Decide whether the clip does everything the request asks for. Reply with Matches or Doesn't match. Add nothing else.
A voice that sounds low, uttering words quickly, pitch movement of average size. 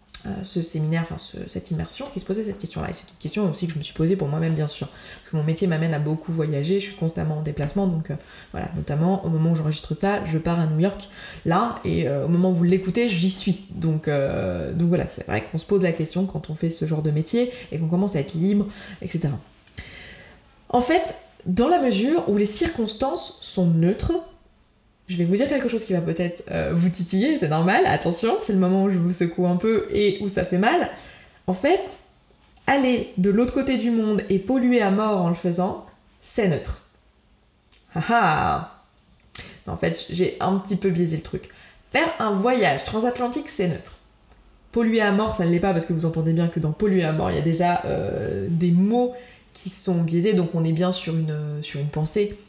Doesn't match